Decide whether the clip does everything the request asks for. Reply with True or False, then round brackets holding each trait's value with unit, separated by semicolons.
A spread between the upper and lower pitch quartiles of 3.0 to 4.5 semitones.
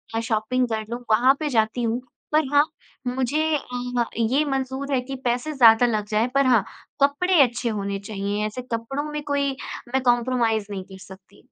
True (3.7 semitones)